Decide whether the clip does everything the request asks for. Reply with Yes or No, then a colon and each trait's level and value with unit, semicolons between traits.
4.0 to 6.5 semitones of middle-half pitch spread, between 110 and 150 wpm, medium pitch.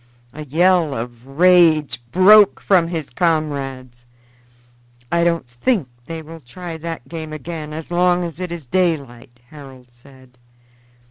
Yes: average, 4.6 semitones; slow, 135 wpm; medium, 155 Hz